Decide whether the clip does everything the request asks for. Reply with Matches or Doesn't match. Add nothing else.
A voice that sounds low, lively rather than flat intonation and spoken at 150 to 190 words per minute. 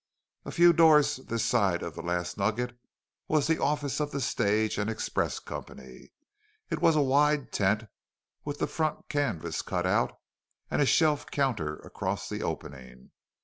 Matches